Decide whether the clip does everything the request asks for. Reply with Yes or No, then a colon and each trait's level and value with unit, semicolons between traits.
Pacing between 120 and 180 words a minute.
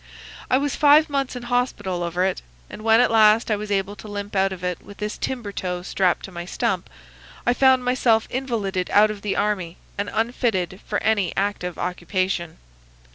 No: average, 190 wpm